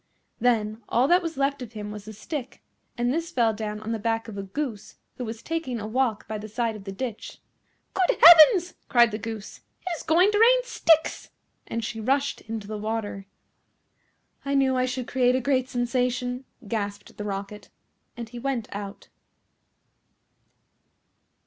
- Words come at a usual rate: Yes, average, 175 wpm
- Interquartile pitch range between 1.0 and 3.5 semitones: No, average, 4.2 semitones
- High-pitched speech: Yes, high, 240 Hz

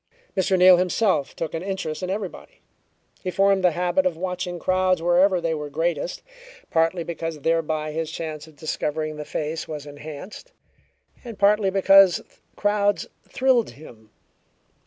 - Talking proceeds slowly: No, average, 145 wpm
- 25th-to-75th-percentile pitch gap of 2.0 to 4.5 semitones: Yes, average, 3.4 semitones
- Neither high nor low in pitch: Yes, medium, 175 Hz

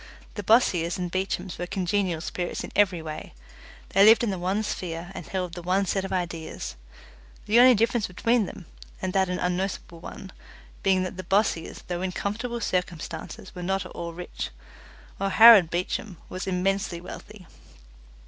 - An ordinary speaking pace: Yes, average, 170 wpm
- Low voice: No, medium, 185 Hz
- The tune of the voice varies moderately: No, narrow, 2.1 semitones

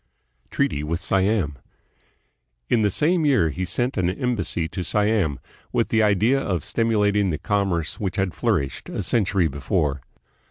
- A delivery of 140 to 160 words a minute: Yes, average, 155 wpm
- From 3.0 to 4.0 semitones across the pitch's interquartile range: No, average, 4.8 semitones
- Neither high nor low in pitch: No, very low, 95 Hz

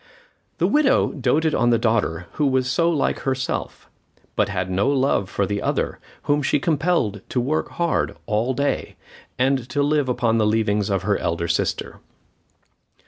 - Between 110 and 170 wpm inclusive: Yes, average, 165 wpm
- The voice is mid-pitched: No, low, 125 Hz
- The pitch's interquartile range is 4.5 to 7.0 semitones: Yes, wide, 5.6 semitones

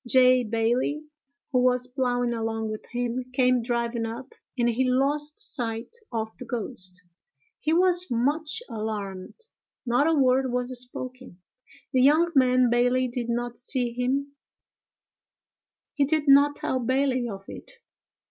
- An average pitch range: No, narrow, 2.3 semitones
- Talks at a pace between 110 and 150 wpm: Yes, average, 140 wpm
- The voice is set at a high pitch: Yes, very high, 250 Hz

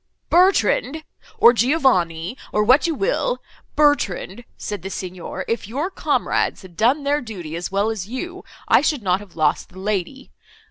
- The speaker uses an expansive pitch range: Yes, wide, 7.6 semitones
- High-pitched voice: Yes, high, 225 Hz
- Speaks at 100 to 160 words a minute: Yes, average, 150 wpm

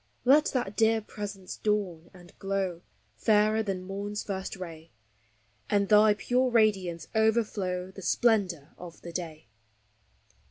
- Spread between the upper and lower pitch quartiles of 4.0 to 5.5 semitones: No, average, 3.1 semitones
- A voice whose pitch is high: Yes, high, 195 Hz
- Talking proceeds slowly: Yes, slow, 125 wpm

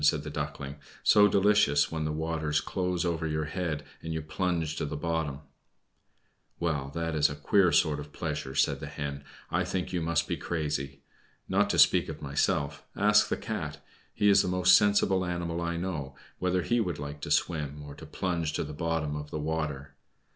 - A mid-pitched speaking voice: No, very low, 80 Hz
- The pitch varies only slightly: No, average, 3.2 semitones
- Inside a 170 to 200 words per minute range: Yes, average, 195 wpm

